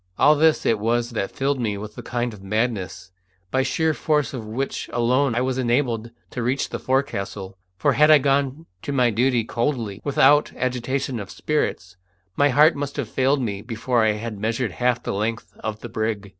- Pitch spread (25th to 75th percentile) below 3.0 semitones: No, average, 3.8 semitones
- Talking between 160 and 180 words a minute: No, average, 200 wpm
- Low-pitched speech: Yes, low, 120 Hz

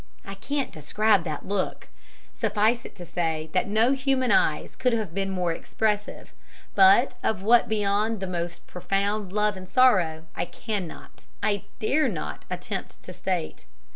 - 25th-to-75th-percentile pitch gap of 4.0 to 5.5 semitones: No, average, 3.6 semitones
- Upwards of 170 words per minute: No, average, 155 wpm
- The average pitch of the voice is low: No, high, 200 Hz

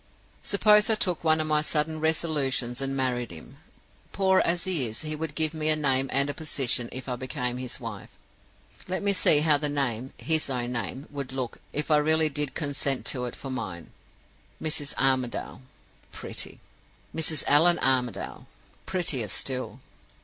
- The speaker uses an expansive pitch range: No, average, 3.6 semitones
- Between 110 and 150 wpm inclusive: No, average, 170 wpm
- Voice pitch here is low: No, medium, 145 Hz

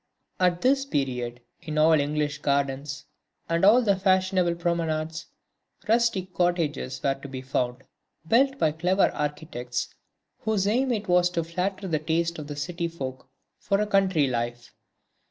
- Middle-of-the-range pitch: Yes, medium, 165 Hz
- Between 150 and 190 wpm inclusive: Yes, average, 155 wpm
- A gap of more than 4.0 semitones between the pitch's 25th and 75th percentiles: Yes, average, 4.9 semitones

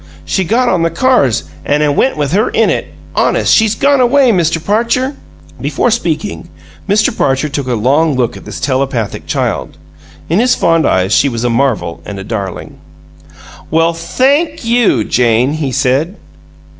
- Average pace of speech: Yes, average, 170 wpm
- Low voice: No, medium, 160 Hz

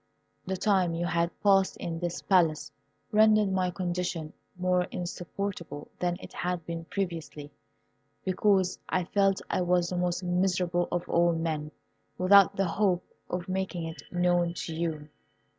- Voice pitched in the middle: Yes, medium, 175 Hz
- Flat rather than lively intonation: Yes, narrow, 1.7 semitones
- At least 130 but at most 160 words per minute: Yes, average, 145 wpm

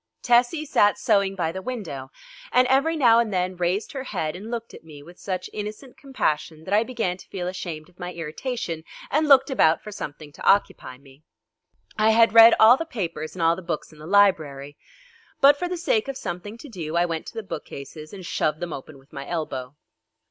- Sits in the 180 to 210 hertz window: Yes, medium, 185 Hz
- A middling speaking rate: No, fast, 215 wpm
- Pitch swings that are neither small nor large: No, wide, 6.6 semitones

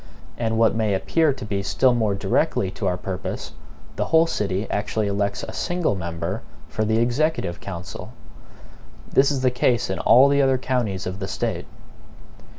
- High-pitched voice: No, low, 110 Hz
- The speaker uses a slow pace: No, average, 170 wpm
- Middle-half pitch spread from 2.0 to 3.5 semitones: No, average, 4.8 semitones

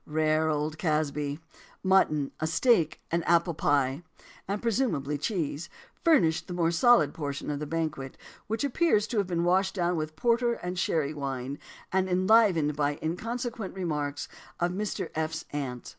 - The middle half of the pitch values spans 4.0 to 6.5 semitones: Yes, average, 4.5 semitones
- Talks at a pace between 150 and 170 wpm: Yes, average, 160 wpm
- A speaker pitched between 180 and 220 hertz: No, medium, 165 Hz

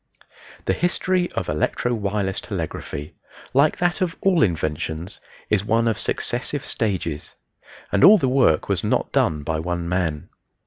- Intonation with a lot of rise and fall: Yes, wide, 8.7 semitones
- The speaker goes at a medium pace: Yes, average, 145 wpm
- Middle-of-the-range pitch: No, low, 100 Hz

